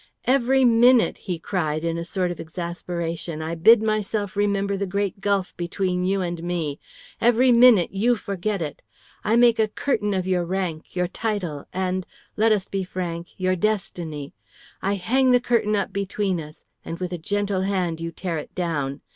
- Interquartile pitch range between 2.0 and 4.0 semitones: Yes, average, 3.6 semitones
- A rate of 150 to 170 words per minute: No, average, 180 wpm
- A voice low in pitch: No, high, 190 Hz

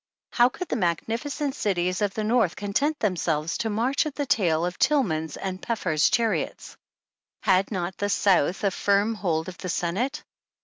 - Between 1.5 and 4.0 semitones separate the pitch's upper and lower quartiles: No, average, 4.9 semitones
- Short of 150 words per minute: No, average, 165 wpm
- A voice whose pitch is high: Yes, high, 200 Hz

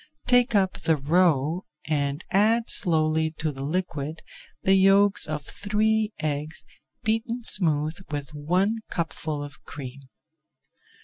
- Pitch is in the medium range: Yes, medium, 160 Hz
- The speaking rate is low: Yes, slow, 120 wpm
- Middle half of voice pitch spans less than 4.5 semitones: No, average, 5.2 semitones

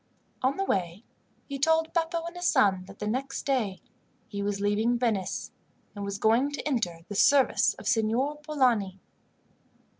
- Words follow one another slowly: No, average, 160 wpm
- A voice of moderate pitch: No, high, 235 Hz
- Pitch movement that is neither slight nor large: No, wide, 5.8 semitones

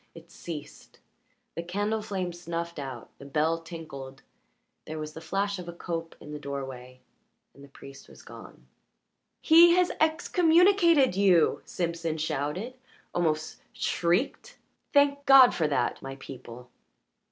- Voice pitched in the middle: Yes, medium, 170 Hz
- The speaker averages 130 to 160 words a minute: Yes, slow, 135 wpm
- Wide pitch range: Yes, wide, 5.8 semitones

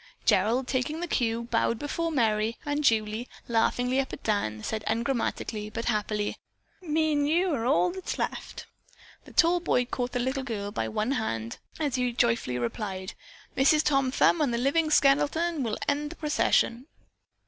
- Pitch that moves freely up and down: No, average, 5.0 semitones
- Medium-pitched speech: No, very high, 250 Hz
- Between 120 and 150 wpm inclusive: No, average, 165 wpm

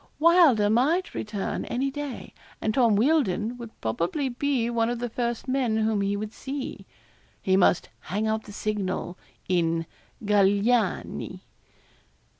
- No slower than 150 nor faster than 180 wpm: No, slow, 135 wpm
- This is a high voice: Yes, high, 225 Hz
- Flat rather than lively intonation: No, average, 4.2 semitones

